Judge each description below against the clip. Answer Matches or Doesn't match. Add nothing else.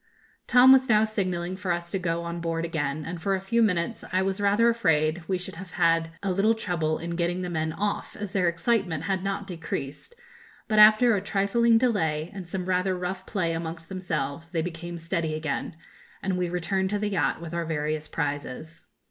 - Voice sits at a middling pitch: Matches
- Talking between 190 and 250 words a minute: Matches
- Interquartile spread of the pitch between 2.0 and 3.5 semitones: Matches